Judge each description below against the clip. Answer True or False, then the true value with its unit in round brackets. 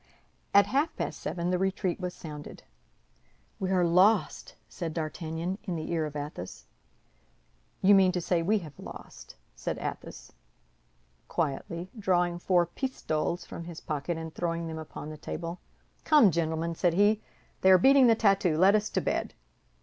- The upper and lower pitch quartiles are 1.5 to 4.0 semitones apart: True (2.9 semitones)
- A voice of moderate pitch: True (175 Hz)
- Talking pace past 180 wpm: False (160 wpm)